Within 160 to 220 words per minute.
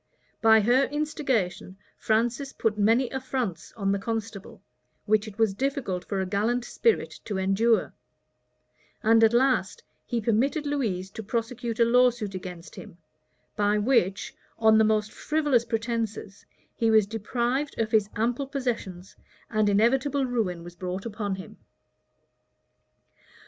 No: slow, 135 wpm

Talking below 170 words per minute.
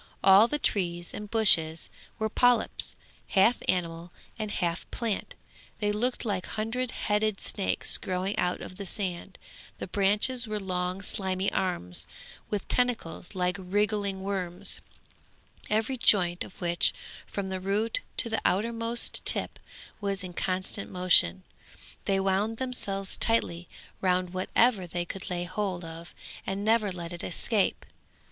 Yes: average, 140 wpm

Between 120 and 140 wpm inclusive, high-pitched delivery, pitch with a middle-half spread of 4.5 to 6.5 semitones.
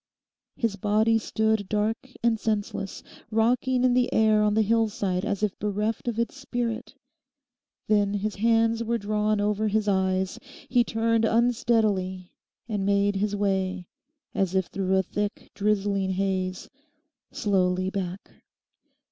No: slow, 135 wpm; high, 210 Hz; narrow, 2.5 semitones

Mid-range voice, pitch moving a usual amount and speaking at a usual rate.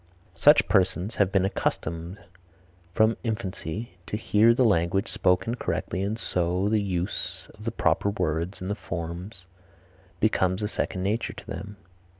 No: very low, 95 Hz; average, 3.3 semitones; average, 145 wpm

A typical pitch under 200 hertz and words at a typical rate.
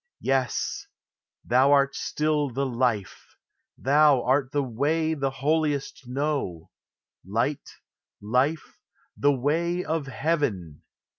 No: medium, 140 Hz; slow, 100 wpm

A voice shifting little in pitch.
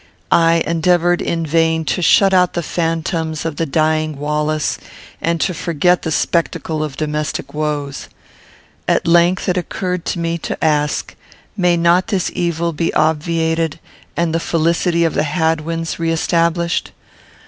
Yes: narrow, 1.6 semitones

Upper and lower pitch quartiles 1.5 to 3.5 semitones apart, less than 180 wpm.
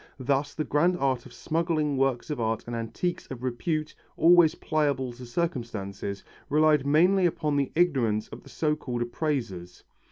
No: average, 4.6 semitones; average, 160 wpm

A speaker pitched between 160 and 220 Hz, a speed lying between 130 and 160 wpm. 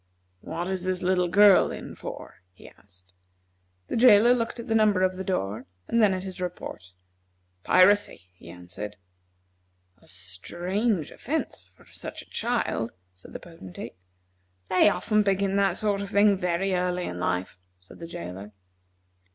Yes: medium, 185 Hz; average, 155 wpm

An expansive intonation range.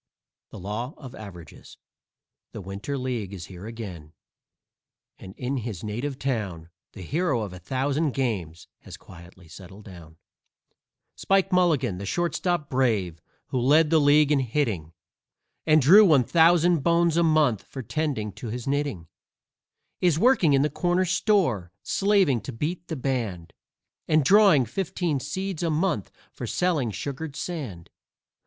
Yes: wide, 7.9 semitones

